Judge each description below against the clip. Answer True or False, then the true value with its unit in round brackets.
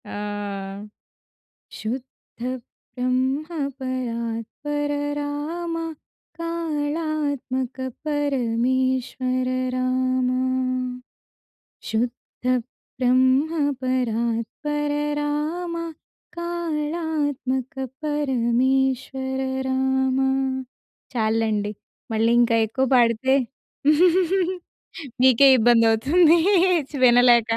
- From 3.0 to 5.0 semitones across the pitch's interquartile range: True (3.4 semitones)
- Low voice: False (260 Hz)